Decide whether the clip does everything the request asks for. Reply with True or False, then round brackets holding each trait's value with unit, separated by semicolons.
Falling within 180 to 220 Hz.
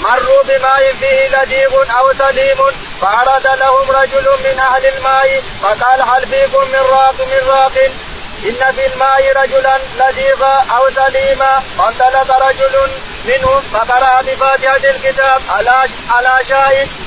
False (270 Hz)